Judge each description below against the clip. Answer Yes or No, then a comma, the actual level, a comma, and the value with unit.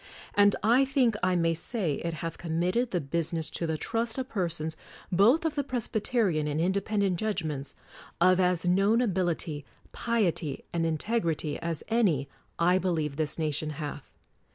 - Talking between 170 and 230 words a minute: No, average, 155 wpm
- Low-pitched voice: No, medium, 175 Hz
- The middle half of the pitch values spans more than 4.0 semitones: Yes, average, 5.3 semitones